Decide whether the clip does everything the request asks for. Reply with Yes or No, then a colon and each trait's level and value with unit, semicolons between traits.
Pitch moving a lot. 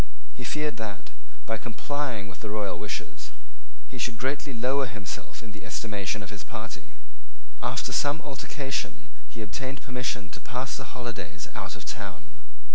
No: average, 4.4 semitones